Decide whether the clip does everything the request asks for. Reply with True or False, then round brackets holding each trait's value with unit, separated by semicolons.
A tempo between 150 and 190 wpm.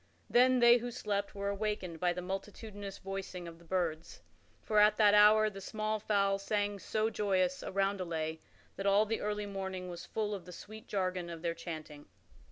True (185 wpm)